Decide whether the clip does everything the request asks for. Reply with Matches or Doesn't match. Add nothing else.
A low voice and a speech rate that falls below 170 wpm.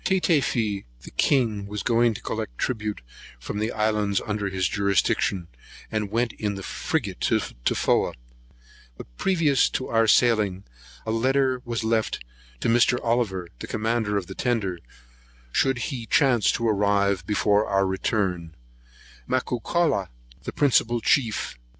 Matches